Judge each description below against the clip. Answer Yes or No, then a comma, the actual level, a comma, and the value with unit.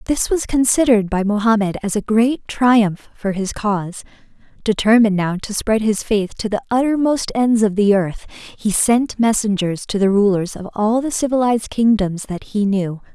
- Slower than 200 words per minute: Yes, average, 180 wpm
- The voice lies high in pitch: Yes, high, 215 Hz